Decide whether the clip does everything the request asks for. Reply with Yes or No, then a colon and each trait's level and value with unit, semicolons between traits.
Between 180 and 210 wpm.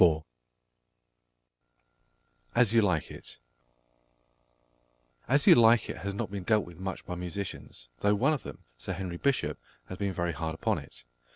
No: average, 155 wpm